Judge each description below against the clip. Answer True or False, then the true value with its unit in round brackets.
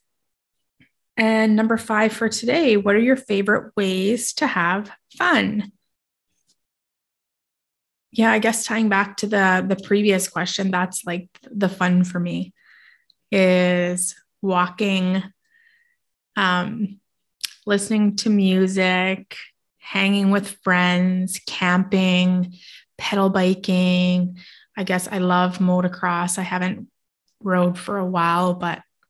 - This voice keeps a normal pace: False (110 wpm)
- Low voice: False (190 Hz)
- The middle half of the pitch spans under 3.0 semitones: True (2.4 semitones)